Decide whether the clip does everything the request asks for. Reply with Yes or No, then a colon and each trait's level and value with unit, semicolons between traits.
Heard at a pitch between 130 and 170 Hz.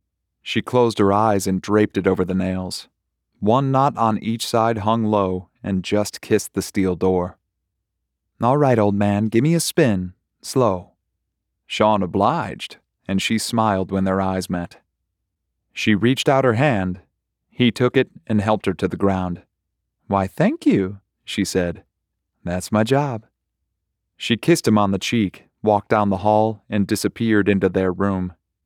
No: low, 100 Hz